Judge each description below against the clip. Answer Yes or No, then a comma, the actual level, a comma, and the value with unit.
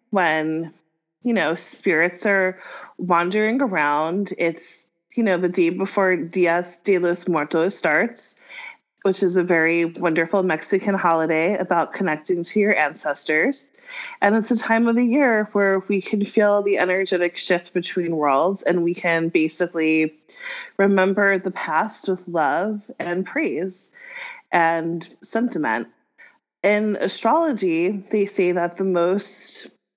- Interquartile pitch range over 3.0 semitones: Yes, average, 3.6 semitones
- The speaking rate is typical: No, slow, 130 wpm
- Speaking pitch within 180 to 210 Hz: Yes, medium, 185 Hz